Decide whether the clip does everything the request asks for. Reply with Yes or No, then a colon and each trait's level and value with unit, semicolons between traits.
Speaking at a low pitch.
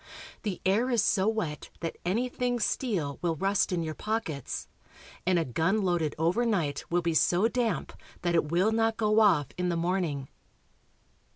No: medium, 180 Hz